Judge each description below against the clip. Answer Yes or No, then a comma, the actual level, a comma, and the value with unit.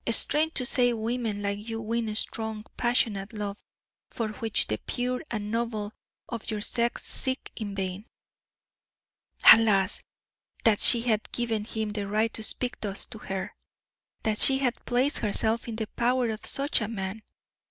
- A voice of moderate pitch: No, high, 220 Hz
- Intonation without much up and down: Yes, narrow, 2.3 semitones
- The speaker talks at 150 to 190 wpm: Yes, average, 160 wpm